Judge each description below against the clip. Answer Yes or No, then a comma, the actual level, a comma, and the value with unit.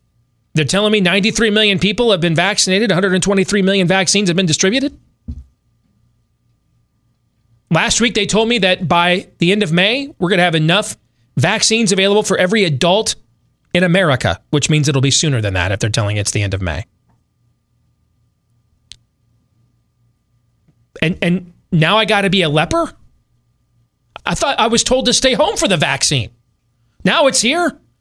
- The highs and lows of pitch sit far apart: Yes, wide, 8.9 semitones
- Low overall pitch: No, medium, 155 Hz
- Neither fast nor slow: Yes, average, 165 wpm